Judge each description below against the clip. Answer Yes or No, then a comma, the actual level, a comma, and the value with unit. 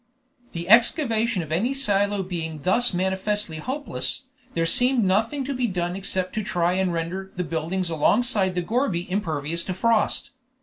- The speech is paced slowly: No, average, 160 wpm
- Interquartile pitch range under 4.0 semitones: No, average, 4.7 semitones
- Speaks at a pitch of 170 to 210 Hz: Yes, high, 190 Hz